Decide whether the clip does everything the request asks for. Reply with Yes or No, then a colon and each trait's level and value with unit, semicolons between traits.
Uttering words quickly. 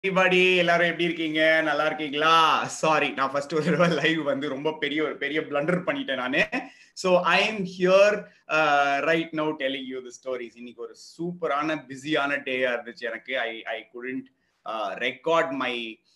Yes: fast, 140 wpm